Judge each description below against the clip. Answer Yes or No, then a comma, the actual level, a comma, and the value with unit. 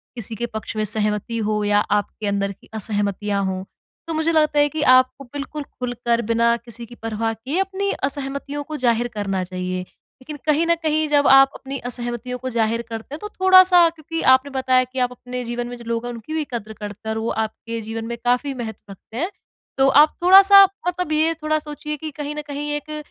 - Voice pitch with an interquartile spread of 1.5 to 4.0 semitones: No, average, 5.2 semitones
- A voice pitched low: No, very high, 250 Hz